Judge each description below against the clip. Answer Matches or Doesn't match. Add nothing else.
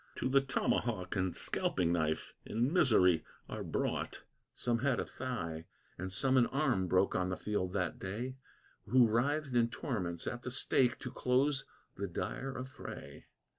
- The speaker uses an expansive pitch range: Matches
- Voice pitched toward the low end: Matches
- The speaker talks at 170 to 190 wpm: Doesn't match